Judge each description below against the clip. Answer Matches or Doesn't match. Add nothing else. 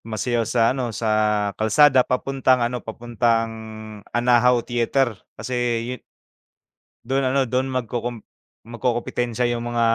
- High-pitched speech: Doesn't match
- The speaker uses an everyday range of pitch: Doesn't match